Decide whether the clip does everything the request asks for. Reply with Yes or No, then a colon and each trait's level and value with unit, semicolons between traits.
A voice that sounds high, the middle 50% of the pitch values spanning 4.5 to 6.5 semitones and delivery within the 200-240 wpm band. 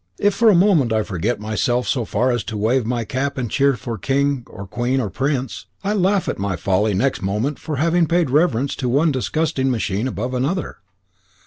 No: low, 130 Hz; average, 4.9 semitones; fast, 205 wpm